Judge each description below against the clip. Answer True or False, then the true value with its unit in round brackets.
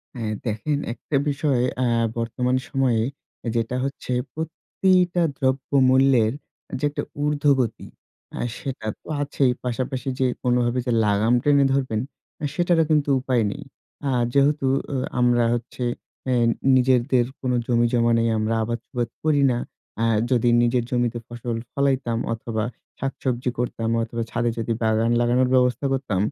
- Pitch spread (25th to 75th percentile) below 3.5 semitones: True (2.6 semitones)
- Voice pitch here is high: False (125 Hz)